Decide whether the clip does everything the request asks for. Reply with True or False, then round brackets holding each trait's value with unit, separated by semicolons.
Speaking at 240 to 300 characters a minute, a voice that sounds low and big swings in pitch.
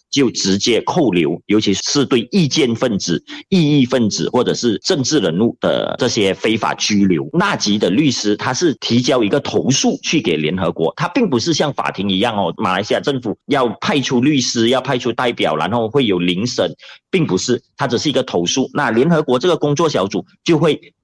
True (295 characters per minute; 125 Hz; 6.2 semitones)